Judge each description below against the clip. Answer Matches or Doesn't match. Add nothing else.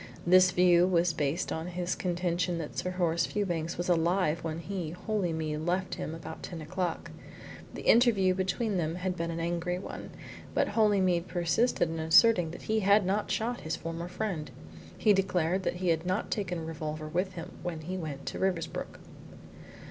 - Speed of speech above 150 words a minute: Matches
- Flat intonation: Matches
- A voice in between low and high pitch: Matches